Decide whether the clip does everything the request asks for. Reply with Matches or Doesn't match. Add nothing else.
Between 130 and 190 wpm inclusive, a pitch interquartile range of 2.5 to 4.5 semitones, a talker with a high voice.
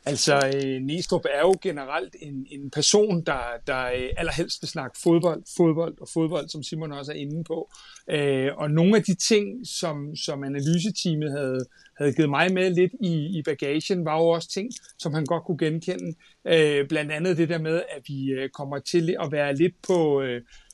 Doesn't match